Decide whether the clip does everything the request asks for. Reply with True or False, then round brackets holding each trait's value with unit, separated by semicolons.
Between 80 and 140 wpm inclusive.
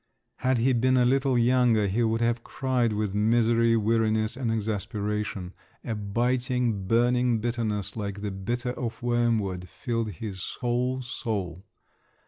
True (135 wpm)